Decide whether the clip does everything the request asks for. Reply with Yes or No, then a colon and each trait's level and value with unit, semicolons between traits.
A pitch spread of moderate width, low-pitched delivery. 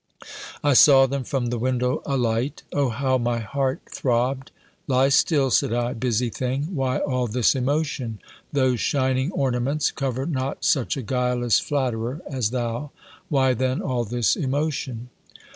No: narrow, 2.1 semitones; low, 130 Hz